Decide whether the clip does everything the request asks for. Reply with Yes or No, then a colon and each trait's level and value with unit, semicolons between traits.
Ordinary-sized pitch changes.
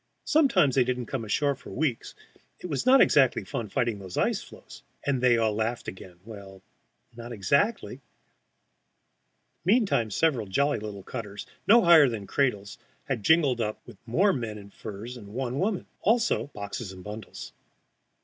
No: wide, 5.7 semitones